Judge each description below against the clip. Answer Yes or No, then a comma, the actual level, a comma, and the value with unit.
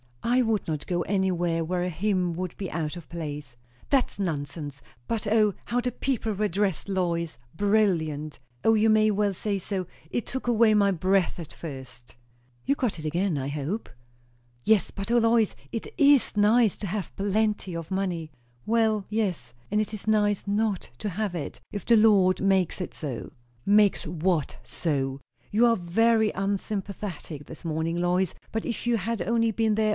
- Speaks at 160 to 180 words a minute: Yes, average, 175 wpm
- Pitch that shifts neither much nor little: Yes, average, 4.3 semitones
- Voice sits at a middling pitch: No, high, 195 Hz